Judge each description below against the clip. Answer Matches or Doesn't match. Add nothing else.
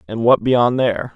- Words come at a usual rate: Doesn't match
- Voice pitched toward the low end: Matches